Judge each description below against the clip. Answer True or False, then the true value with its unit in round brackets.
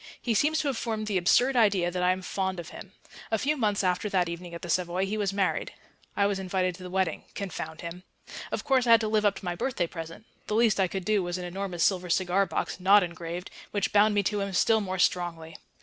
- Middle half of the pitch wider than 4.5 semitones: False (3.0 semitones)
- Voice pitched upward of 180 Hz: True (190 Hz)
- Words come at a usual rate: False (250 wpm)